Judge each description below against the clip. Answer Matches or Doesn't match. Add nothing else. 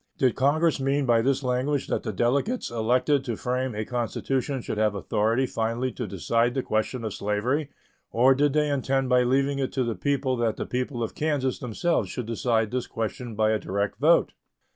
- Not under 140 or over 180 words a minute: Doesn't match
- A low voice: Matches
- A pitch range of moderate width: Matches